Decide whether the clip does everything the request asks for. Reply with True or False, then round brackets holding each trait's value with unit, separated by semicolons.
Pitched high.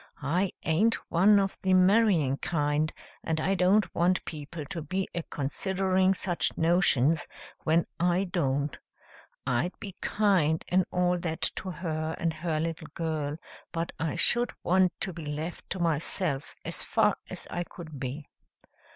False (170 Hz)